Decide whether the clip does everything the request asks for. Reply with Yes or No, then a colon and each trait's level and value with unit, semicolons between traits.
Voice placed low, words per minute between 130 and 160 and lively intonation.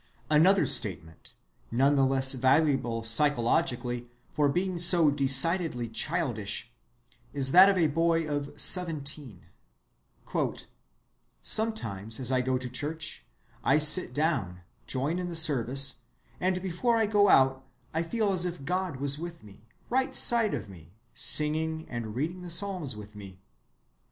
No: medium, 145 Hz; average, 140 wpm; wide, 5.8 semitones